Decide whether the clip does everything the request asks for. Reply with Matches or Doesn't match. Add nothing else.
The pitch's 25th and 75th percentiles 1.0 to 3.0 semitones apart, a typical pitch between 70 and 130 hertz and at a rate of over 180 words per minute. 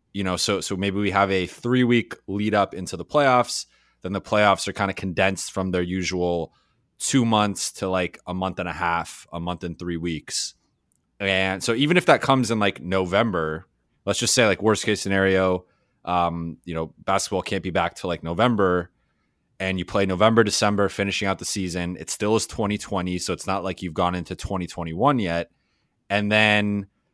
Matches